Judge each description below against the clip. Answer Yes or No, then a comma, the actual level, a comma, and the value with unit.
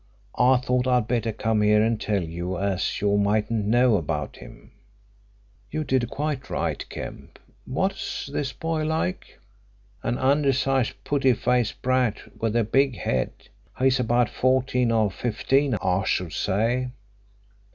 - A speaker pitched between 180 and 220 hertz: No, low, 120 Hz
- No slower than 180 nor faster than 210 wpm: No, average, 140 wpm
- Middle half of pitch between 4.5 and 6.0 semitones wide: No, average, 3.9 semitones